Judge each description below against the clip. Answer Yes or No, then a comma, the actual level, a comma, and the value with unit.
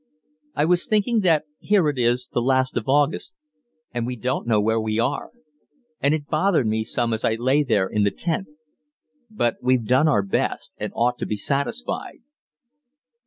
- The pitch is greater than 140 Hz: No, low, 125 Hz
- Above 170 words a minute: Yes, average, 180 wpm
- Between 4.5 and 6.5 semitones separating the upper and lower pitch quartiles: Yes, average, 5.2 semitones